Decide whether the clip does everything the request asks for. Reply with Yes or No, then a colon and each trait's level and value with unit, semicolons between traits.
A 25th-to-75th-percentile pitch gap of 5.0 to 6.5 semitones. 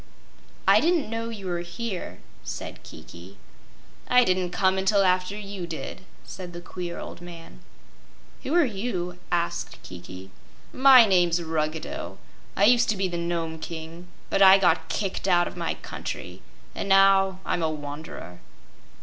No: average, 2.8 semitones